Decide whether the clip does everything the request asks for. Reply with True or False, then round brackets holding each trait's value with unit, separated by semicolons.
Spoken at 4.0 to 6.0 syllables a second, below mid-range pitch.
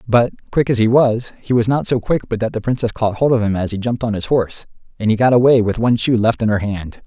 False (6.2 syllables/s; 115 Hz)